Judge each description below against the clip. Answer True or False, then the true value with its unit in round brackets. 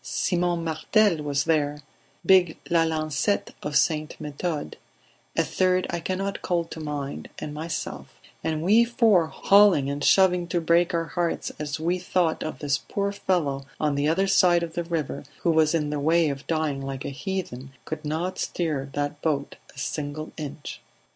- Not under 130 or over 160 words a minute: False (170 wpm)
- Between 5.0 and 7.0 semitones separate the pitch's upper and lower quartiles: False (3.2 semitones)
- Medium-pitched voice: True (160 Hz)